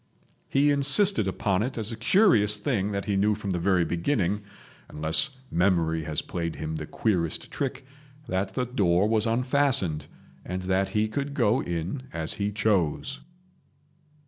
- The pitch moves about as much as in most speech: No, wide, 6.6 semitones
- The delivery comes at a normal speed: Yes, average, 145 wpm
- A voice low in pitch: Yes, low, 105 Hz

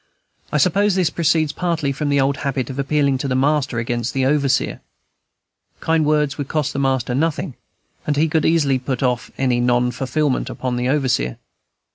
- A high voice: No, medium, 140 Hz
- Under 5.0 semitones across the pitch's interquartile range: Yes, average, 2.8 semitones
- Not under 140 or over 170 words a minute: No, average, 180 wpm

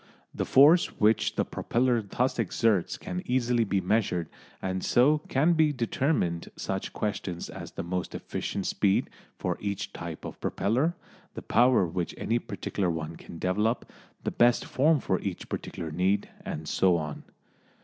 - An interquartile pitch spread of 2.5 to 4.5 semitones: No, wide, 5.4 semitones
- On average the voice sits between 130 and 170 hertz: No, low, 105 Hz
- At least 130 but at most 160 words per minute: Yes, average, 155 wpm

